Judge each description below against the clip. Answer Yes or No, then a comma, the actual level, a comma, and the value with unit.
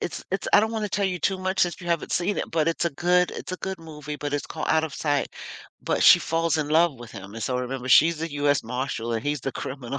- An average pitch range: Yes, average, 4.2 semitones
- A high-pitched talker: No, medium, 155 Hz